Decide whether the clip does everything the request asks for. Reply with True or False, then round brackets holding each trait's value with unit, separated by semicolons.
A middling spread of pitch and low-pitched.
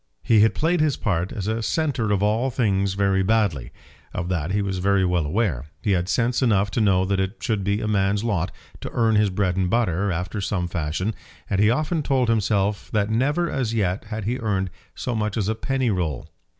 True (3.3 semitones; 105 Hz)